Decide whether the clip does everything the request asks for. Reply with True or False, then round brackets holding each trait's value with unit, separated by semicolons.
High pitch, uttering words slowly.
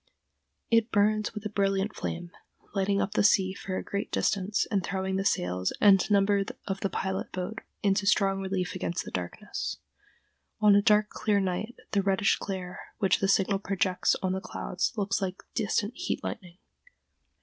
False (195 Hz; 170 wpm)